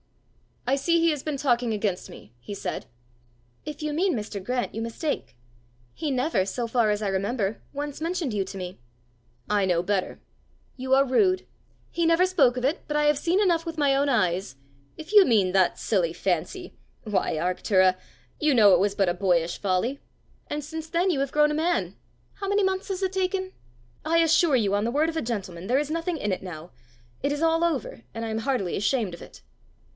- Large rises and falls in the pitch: Yes, wide, 8.4 semitones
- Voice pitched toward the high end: Yes, very high, 255 Hz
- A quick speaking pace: Yes, fast, 210 wpm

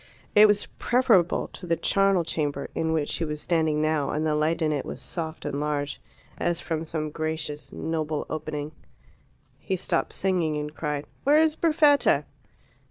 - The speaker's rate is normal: Yes, average, 165 wpm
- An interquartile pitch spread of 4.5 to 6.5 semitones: No, average, 3.1 semitones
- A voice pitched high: No, medium, 160 Hz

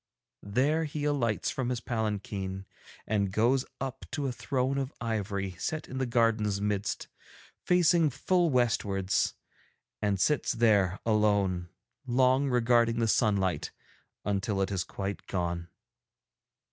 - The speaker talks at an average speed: No, slow, 125 wpm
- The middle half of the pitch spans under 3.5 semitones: No, average, 4.7 semitones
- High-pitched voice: No, low, 115 Hz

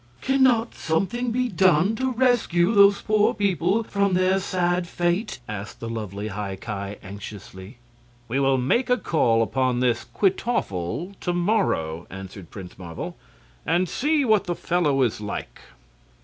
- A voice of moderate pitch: Yes, medium, 175 Hz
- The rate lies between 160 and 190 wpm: No, average, 150 wpm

